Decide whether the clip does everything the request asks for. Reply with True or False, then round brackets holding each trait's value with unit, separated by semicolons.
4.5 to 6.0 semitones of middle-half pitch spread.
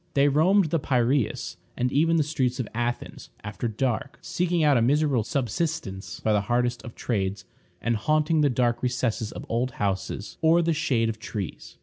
True (5.1 semitones)